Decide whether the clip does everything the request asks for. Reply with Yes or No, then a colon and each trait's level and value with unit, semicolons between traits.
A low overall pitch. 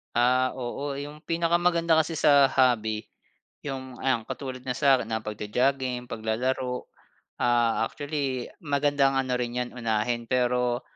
Yes: low, 130 Hz